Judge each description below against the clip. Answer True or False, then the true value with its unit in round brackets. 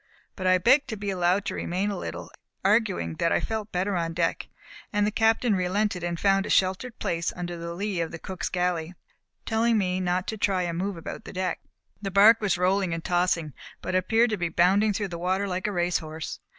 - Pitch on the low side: False (185 Hz)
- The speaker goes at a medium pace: False (220 wpm)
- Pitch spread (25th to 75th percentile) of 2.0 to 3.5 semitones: True (2.8 semitones)